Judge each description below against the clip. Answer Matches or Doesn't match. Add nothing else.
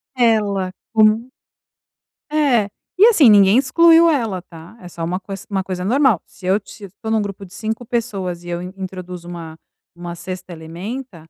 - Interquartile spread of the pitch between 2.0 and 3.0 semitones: Doesn't match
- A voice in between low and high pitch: Doesn't match